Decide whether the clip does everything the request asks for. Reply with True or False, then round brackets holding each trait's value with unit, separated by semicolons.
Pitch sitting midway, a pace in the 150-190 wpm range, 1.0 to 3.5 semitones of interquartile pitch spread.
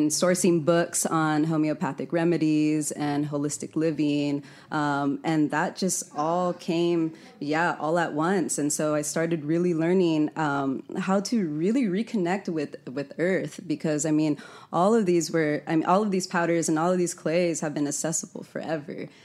True (160 Hz; 170 wpm; 2.7 semitones)